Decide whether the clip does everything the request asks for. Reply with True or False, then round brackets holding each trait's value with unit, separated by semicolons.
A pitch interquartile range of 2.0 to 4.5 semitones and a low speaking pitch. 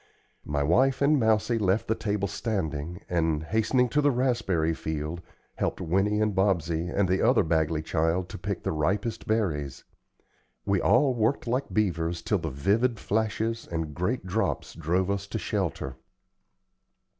False (5.3 semitones; 95 Hz)